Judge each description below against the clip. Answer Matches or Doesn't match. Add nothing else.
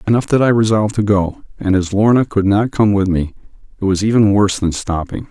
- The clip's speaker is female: Doesn't match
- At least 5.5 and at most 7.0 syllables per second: Matches